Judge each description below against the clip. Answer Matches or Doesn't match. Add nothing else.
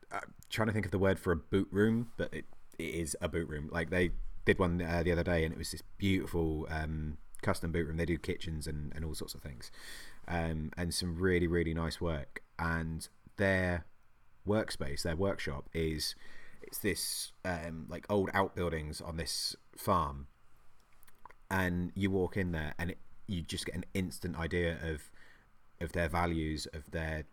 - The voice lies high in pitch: Doesn't match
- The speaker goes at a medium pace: Matches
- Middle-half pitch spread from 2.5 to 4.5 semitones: Matches